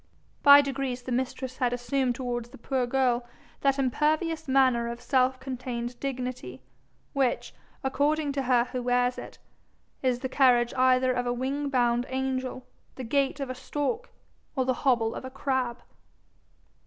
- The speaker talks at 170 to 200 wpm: No, average, 155 wpm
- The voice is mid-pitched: No, very high, 255 Hz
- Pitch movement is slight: Yes, narrow, 1.7 semitones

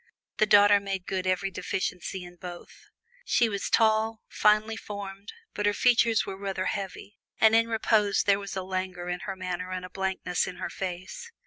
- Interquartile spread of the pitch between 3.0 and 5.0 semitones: No, narrow, 2.4 semitones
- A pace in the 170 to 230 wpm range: Yes, average, 185 wpm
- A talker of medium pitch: No, high, 195 Hz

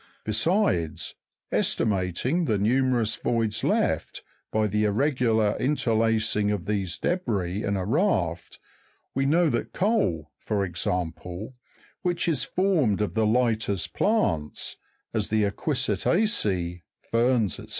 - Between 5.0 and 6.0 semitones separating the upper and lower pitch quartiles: Yes, wide, 5.4 semitones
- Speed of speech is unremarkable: No, slow, 115 wpm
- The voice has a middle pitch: No, low, 110 Hz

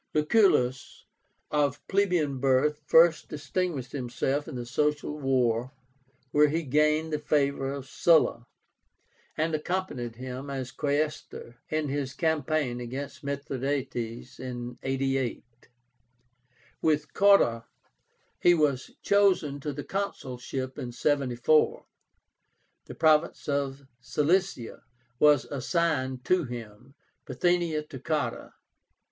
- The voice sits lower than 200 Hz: Yes, medium, 140 Hz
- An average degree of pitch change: Yes, average, 3.1 semitones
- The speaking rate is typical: No, slow, 105 wpm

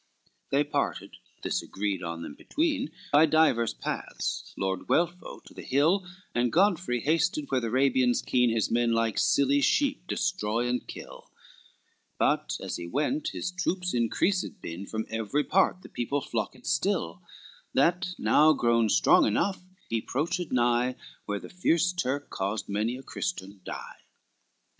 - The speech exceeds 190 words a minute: No, average, 150 wpm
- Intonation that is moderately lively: No, wide, 7.4 semitones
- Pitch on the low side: Yes, low, 130 Hz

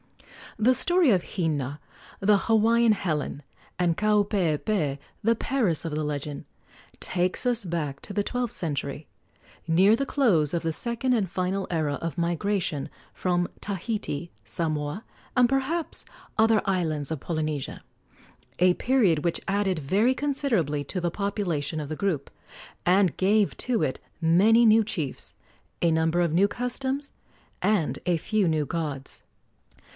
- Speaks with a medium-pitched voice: Yes, medium, 180 Hz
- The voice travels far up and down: Yes, wide, 5.7 semitones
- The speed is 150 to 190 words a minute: No, average, 140 wpm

